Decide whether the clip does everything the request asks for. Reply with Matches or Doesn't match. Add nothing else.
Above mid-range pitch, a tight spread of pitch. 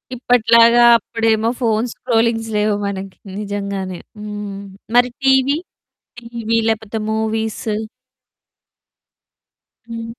Matches